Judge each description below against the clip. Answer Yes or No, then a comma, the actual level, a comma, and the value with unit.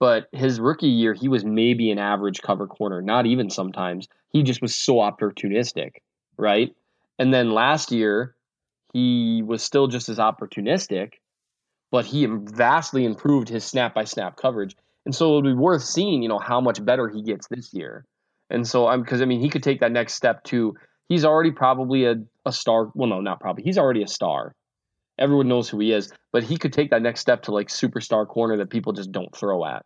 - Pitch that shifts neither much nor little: Yes, average, 3.2 semitones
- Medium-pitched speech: No, low, 120 Hz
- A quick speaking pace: Yes, fast, 210 wpm